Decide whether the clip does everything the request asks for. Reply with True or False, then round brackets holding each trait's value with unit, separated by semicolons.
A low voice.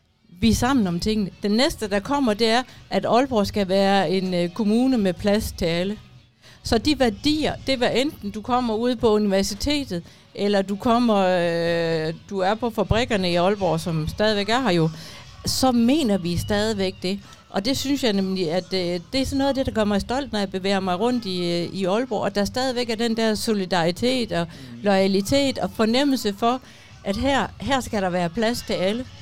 False (205 Hz)